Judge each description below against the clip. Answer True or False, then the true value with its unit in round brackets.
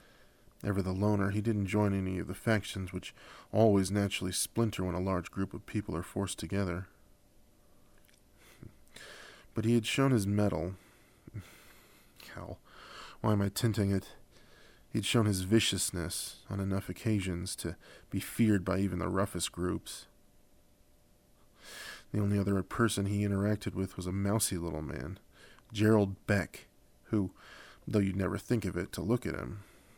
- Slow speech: False (150 wpm)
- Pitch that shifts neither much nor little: False (2.1 semitones)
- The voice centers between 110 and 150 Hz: False (100 Hz)